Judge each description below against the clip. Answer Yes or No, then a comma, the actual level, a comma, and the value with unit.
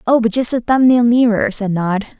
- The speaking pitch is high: Yes, high, 230 Hz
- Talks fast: Yes, fast, 245 wpm